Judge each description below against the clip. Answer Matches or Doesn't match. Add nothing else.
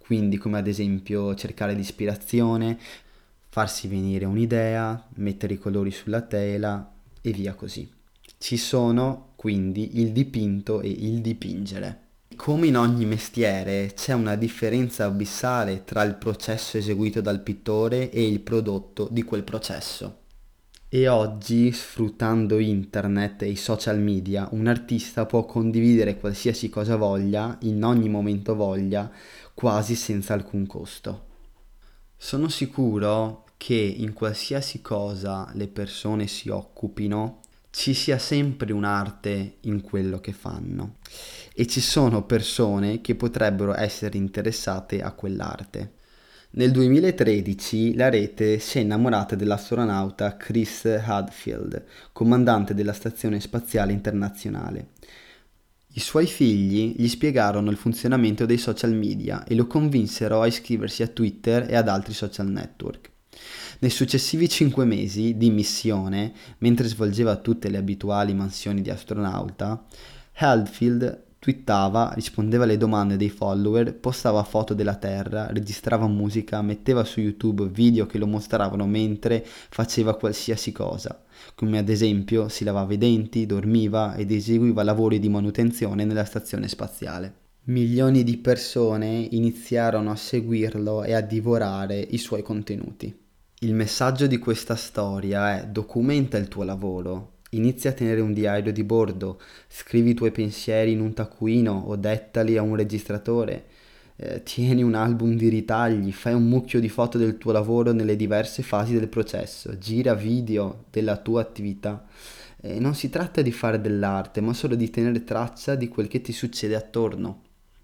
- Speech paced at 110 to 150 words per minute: Matches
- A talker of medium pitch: Doesn't match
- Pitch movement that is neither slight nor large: Doesn't match